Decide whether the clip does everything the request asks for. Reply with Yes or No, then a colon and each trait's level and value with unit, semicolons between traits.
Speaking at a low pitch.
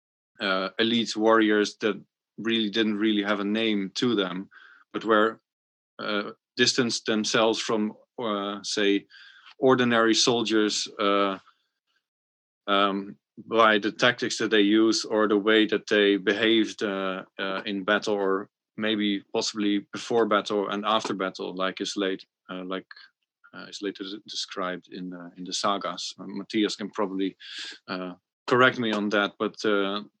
Yes: low, 105 Hz